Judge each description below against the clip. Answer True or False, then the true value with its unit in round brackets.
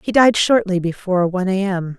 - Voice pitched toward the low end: False (190 Hz)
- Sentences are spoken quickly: True (210 wpm)